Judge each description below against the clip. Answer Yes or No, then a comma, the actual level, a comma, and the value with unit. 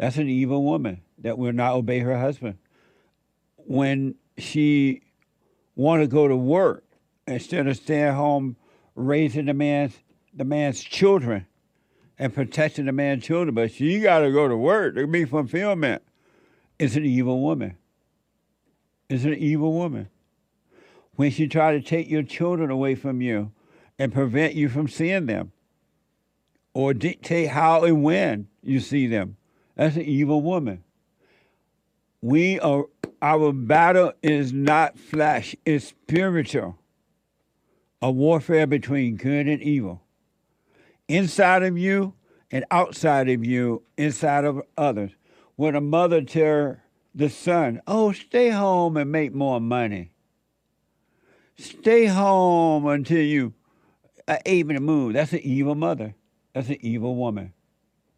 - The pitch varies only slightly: No, average, 3.5 semitones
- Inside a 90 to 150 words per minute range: Yes, slow, 135 wpm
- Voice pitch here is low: No, medium, 145 Hz